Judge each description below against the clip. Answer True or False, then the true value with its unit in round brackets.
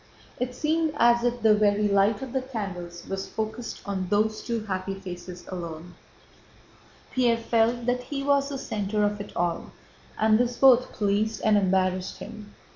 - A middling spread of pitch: True (3.8 semitones)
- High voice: True (215 Hz)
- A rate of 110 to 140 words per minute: False (165 wpm)